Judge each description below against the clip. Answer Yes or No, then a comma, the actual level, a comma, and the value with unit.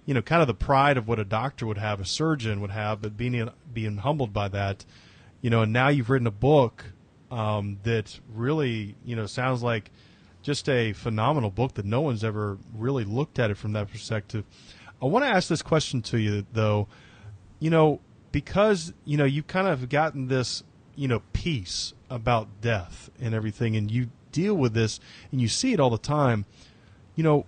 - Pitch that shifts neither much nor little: Yes, average, 4.6 semitones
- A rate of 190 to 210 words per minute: Yes, average, 200 wpm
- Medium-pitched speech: No, low, 120 Hz